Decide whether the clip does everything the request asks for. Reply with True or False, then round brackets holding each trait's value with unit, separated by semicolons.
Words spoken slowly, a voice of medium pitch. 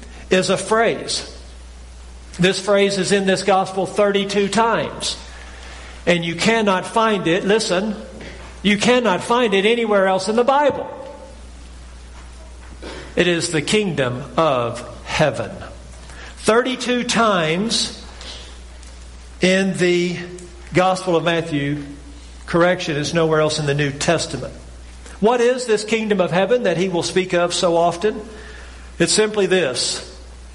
True (125 wpm; 175 Hz)